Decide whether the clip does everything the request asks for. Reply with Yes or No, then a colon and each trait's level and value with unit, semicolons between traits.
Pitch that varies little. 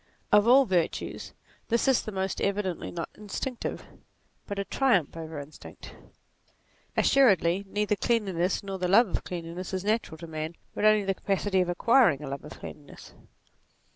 No: average, 3.9 semitones